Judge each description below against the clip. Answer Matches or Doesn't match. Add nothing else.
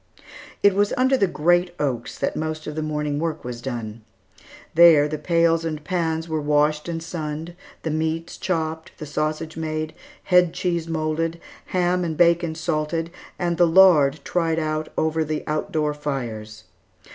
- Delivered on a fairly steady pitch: Matches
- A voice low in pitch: Doesn't match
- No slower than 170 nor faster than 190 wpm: Doesn't match